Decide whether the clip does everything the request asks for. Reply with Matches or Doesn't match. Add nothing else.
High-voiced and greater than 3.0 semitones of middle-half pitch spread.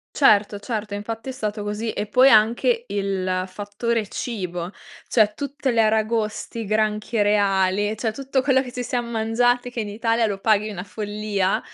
Doesn't match